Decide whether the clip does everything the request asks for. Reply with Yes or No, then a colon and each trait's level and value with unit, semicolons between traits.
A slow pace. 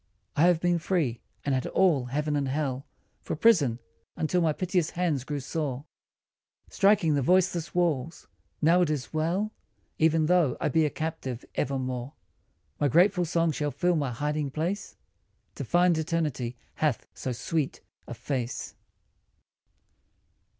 No: average, 145 wpm